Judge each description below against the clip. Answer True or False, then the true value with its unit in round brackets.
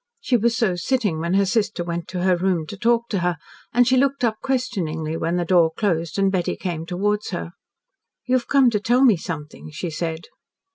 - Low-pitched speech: False (190 Hz)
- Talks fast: True (210 wpm)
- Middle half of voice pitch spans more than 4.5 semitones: True (5.5 semitones)